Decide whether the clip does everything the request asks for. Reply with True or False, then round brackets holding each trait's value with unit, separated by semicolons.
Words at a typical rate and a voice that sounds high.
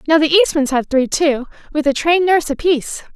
False (210 wpm; 300 Hz)